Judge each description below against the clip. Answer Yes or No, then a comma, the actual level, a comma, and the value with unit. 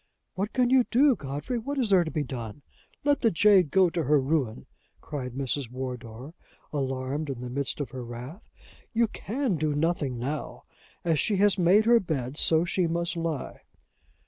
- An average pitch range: No, wide, 6.8 semitones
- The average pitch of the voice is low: No, medium, 155 Hz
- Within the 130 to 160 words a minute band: No, average, 180 wpm